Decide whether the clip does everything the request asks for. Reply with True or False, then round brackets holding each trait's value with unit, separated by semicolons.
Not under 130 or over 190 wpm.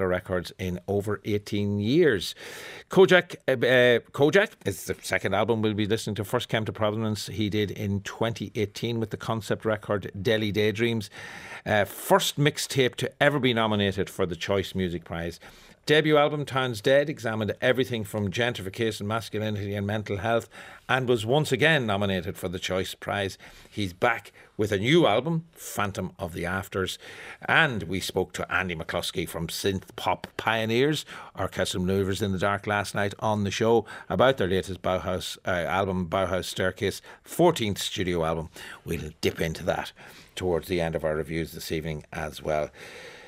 True (165 wpm)